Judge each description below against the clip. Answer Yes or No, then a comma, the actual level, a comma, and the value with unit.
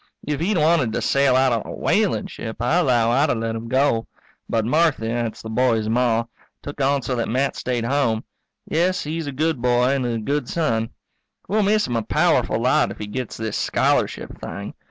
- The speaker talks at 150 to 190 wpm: No, fast, 205 wpm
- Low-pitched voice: Yes, low, 125 Hz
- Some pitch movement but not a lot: Yes, average, 4.2 semitones